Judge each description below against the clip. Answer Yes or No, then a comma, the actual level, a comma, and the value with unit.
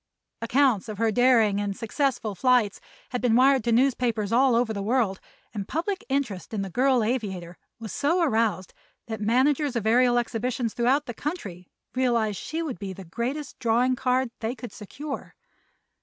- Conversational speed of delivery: Yes, average, 170 wpm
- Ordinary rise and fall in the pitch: Yes, average, 3.4 semitones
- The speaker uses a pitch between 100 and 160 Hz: No, high, 240 Hz